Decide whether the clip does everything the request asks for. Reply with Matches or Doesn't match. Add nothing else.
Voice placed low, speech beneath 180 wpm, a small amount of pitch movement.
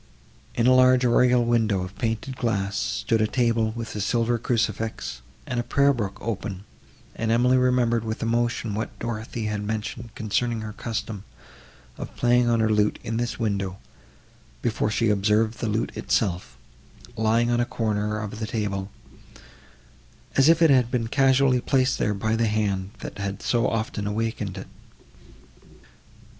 Matches